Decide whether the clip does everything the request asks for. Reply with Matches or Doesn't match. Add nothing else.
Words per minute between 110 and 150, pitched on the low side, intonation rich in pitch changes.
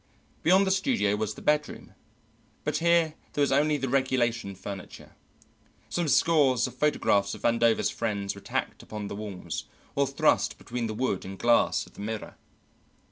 Doesn't match